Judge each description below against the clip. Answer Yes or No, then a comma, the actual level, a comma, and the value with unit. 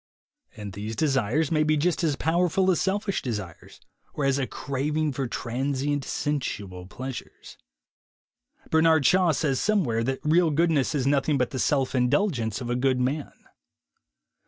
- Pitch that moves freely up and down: No, average, 3.9 semitones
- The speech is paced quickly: No, average, 160 wpm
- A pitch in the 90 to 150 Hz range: Yes, medium, 140 Hz